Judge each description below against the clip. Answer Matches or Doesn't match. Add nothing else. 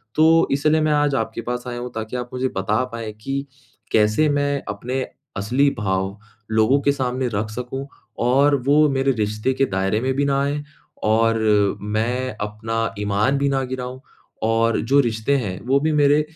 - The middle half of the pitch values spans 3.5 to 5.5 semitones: Matches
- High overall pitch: Doesn't match